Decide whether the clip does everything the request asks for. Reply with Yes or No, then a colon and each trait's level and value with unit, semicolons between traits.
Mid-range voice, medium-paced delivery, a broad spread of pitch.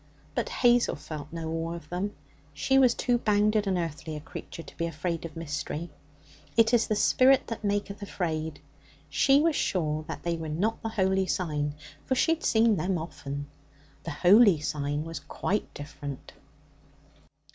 Yes: medium, 175 Hz; average, 170 wpm; wide, 5.8 semitones